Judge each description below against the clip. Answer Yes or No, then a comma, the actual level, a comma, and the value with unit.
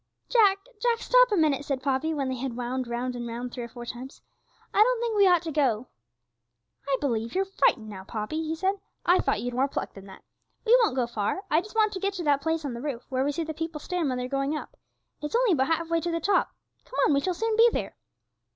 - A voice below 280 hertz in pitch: No, very high, 300 Hz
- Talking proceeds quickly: Yes, fast, 260 wpm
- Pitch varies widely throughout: Yes, wide, 7.0 semitones